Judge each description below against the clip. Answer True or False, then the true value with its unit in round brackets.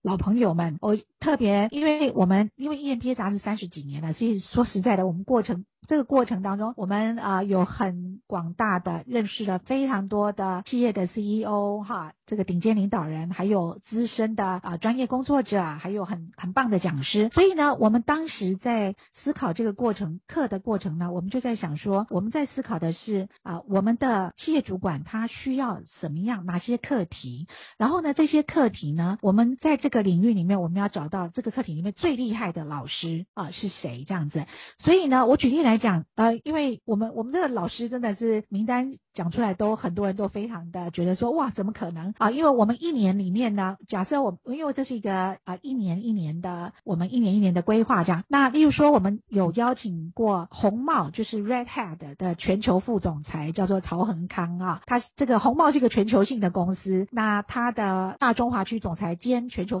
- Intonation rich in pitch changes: False (4.6 semitones)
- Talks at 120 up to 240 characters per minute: False (325 characters per minute)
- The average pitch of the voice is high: True (210 Hz)